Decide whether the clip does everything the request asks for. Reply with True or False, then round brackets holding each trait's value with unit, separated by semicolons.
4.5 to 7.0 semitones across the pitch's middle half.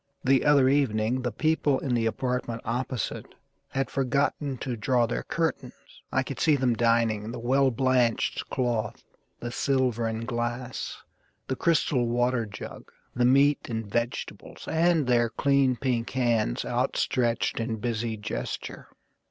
False (2.4 semitones)